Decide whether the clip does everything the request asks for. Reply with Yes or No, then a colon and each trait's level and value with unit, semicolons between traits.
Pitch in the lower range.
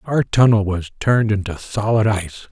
Yes: low, 105 Hz